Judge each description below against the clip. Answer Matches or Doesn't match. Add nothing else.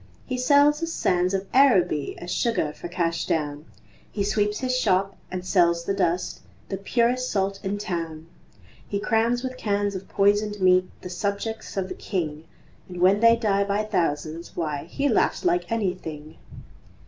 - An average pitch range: Matches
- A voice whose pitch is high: Matches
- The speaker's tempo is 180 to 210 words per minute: Doesn't match